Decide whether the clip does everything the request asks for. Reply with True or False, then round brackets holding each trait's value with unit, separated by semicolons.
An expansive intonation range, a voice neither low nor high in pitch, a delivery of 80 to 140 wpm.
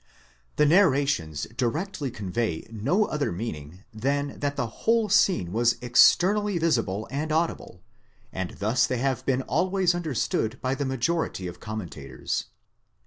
False (6.9 semitones; 130 Hz; 135 wpm)